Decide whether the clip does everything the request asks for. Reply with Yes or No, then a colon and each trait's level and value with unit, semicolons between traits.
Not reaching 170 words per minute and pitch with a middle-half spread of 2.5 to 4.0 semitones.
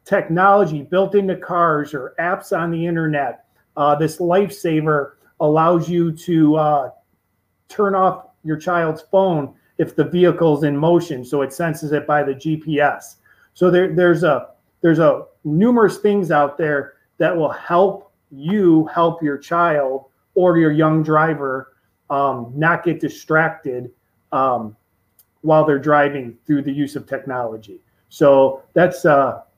Yes: average, 140 wpm; average, 3.4 semitones